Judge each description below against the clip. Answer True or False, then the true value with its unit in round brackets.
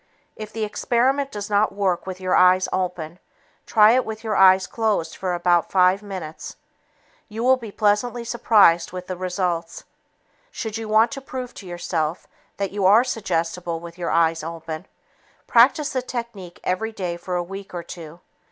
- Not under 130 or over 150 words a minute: False (170 wpm)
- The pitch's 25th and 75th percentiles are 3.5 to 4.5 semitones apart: True (4.2 semitones)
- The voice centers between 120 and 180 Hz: False (190 Hz)